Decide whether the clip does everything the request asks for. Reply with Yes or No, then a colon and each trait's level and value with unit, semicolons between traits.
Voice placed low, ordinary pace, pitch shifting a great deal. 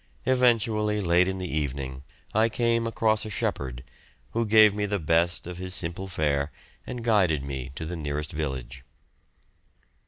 Yes: very low, 90 Hz; average, 155 wpm; wide, 6.7 semitones